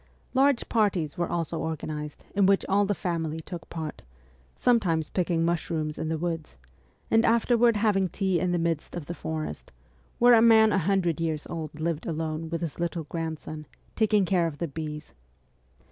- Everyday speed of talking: Yes, average, 175 wpm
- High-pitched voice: No, medium, 170 Hz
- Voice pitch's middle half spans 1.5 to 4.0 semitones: Yes, average, 3.6 semitones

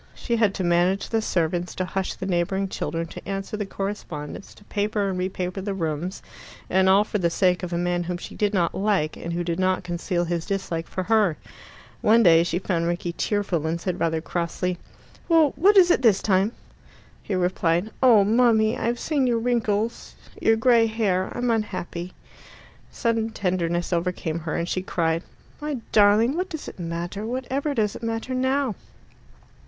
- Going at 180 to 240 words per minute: Yes, average, 185 wpm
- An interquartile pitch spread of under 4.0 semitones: No, average, 4.3 semitones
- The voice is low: No, high, 190 Hz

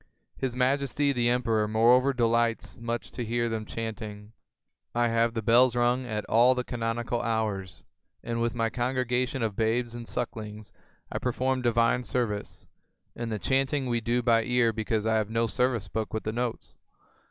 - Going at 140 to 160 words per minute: No, average, 170 wpm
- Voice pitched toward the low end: Yes, low, 115 Hz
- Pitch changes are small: Yes, narrow, 1.8 semitones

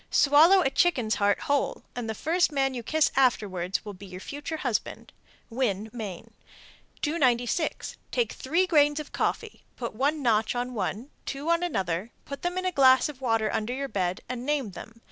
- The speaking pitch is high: Yes, very high, 255 Hz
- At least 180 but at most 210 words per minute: Yes, average, 185 wpm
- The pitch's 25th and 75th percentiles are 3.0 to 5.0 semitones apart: No, wide, 5.4 semitones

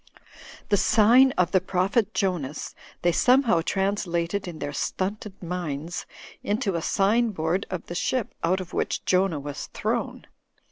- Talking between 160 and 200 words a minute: No, average, 145 wpm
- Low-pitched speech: No, medium, 185 Hz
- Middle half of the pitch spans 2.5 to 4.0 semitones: Yes, average, 3.3 semitones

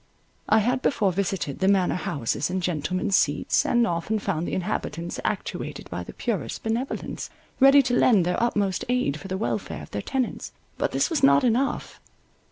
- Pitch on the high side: Yes, high, 195 Hz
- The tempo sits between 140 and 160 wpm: No, average, 175 wpm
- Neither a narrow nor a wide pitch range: No, wide, 5.7 semitones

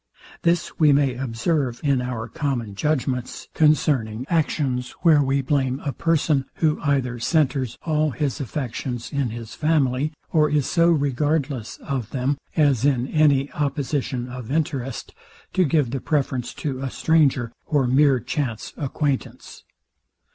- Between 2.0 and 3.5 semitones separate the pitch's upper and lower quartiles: Yes, average, 3.2 semitones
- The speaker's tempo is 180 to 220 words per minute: No, average, 140 wpm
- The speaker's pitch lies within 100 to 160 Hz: Yes, medium, 140 Hz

